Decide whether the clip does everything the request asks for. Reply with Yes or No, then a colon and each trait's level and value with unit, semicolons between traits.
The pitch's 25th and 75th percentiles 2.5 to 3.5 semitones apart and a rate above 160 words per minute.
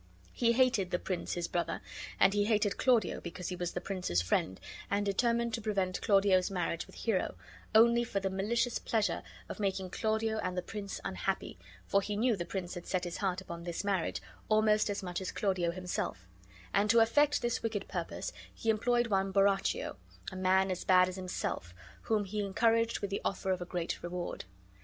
Yes: average, 3.2 semitones; average, 195 wpm